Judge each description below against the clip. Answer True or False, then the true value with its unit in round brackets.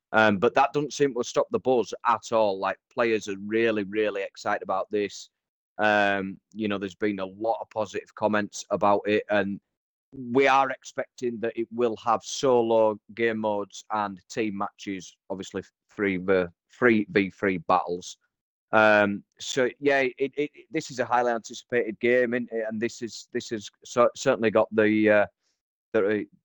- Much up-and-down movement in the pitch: False (2.9 semitones)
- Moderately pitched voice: False (110 Hz)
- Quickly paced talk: False (175 wpm)